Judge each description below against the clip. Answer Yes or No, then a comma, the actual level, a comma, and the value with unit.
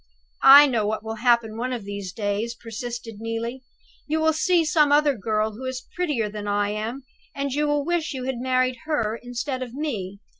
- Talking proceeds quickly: No, average, 195 wpm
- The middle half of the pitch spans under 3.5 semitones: No, average, 4.5 semitones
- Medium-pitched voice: No, high, 245 Hz